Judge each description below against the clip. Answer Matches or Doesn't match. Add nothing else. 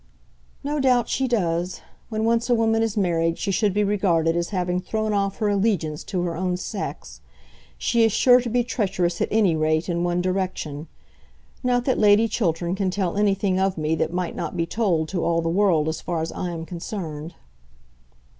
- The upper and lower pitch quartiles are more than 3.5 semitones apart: Matches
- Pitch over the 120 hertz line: Matches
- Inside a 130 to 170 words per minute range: Doesn't match